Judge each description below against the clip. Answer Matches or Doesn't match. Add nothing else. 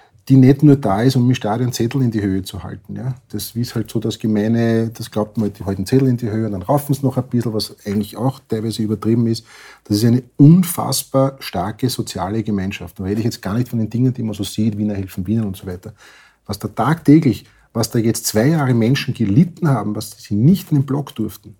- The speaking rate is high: Matches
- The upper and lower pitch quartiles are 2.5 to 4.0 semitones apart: Matches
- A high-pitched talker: Doesn't match